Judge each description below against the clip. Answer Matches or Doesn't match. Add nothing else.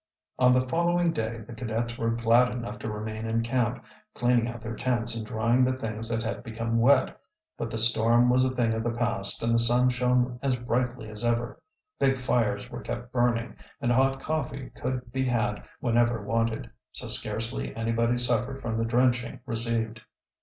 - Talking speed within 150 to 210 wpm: Matches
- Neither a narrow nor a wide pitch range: Doesn't match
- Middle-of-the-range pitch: Doesn't match